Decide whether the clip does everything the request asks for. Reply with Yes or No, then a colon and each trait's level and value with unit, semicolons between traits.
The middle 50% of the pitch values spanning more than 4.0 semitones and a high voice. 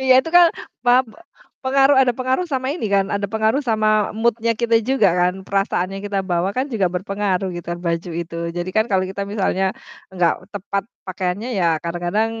Yes: average, 4.7 semitones; high, 205 Hz